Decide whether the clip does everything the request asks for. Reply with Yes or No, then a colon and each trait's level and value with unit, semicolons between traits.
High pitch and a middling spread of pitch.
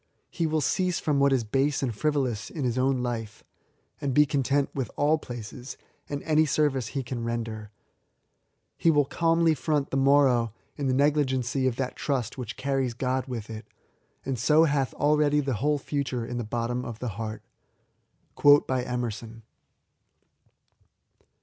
No: low, 130 Hz; average, 3.4 semitones